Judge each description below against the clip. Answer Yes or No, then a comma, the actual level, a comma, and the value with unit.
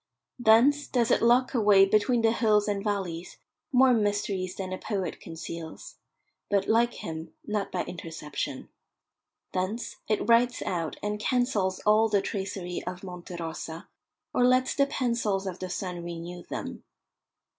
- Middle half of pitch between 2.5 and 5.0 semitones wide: Yes, average, 4.5 semitones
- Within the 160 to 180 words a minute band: No, average, 145 wpm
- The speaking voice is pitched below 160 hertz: No, high, 205 Hz